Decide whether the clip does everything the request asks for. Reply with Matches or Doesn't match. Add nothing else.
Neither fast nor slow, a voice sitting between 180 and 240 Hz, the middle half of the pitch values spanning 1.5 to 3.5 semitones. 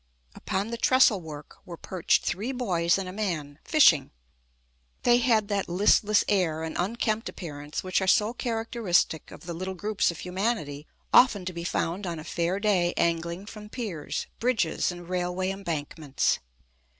Doesn't match